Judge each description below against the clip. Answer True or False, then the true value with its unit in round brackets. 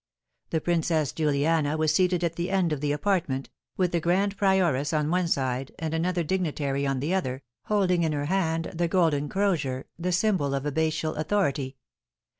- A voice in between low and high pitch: True (160 Hz)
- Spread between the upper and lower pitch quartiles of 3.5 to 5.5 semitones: True (3.9 semitones)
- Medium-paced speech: True (175 wpm)